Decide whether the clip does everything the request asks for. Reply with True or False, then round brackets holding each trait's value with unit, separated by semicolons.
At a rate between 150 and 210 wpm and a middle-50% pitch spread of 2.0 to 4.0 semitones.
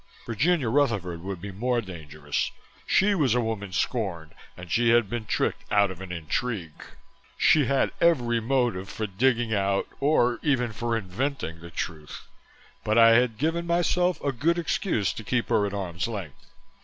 False (170 wpm; 5.4 semitones)